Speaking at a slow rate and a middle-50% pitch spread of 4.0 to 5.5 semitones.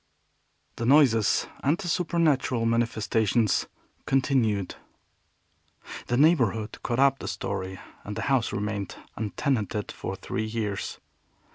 Yes: slow, 105 wpm; average, 4.4 semitones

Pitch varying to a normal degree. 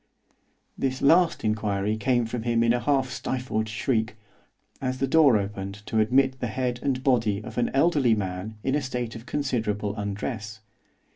Yes: average, 3.5 semitones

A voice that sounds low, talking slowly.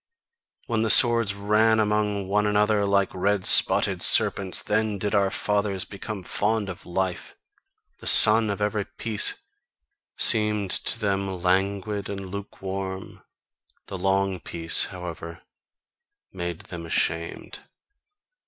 Yes: low, 100 Hz; slow, 120 wpm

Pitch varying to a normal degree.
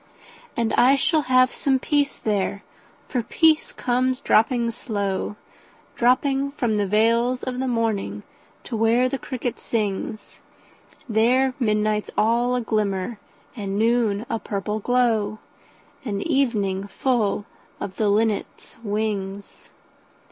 Yes: average, 3.4 semitones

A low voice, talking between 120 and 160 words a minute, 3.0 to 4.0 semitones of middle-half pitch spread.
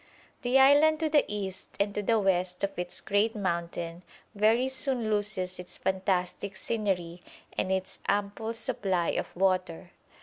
No: high, 200 Hz; average, 145 wpm; average, 3.5 semitones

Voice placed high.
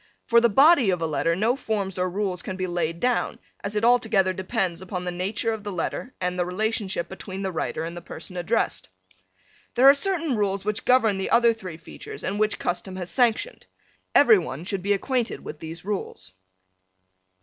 Yes: high, 195 Hz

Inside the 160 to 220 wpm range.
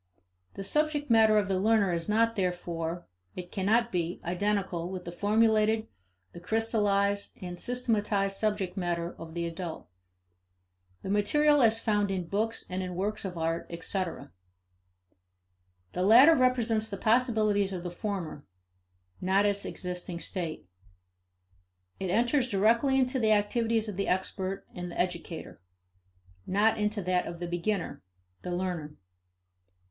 No: average, 140 wpm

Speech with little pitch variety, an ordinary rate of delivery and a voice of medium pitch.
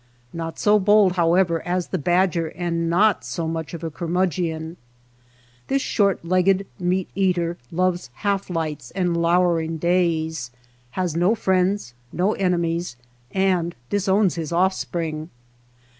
No: narrow, 2.3 semitones; slow, 130 wpm; medium, 175 Hz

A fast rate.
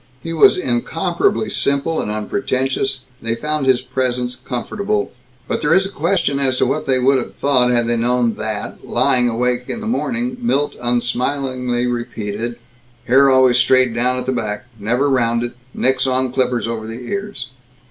No: average, 170 wpm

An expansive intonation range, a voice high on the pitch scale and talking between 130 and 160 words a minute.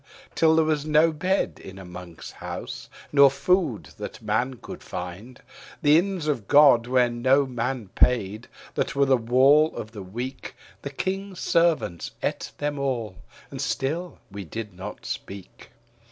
No: wide, 5.9 semitones; low, 130 Hz; average, 155 wpm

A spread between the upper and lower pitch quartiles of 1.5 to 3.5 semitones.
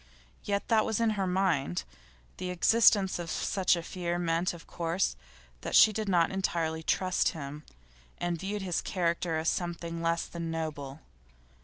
Yes: narrow, 2.6 semitones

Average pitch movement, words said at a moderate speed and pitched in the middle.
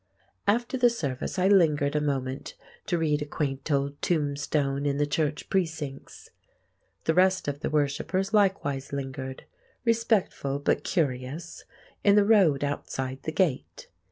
No: average, 5.0 semitones; slow, 130 wpm; medium, 150 Hz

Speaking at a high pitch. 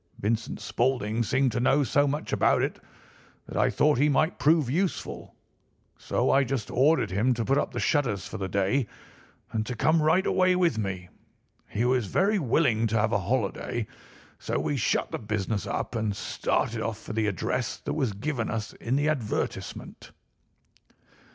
No: low, 120 Hz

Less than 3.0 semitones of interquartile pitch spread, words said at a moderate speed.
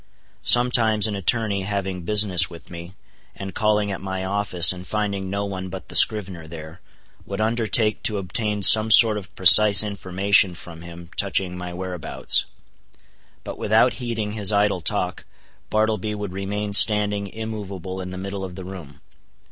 Yes: narrow, 2.5 semitones; average, 155 wpm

